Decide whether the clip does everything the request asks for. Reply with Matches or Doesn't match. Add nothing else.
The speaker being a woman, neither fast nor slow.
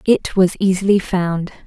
Matches